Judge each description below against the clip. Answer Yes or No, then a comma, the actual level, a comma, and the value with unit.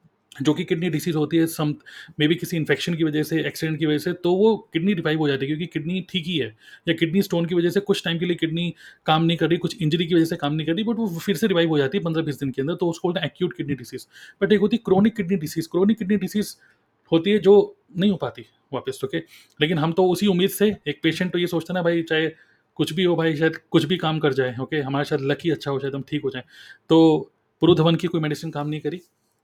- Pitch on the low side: No, medium, 165 Hz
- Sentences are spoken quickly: Yes, fast, 285 wpm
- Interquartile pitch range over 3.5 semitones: No, average, 3.1 semitones